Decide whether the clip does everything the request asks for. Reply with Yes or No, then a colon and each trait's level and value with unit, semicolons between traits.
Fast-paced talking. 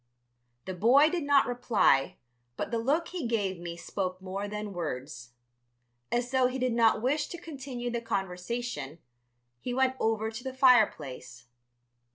No: average, 155 wpm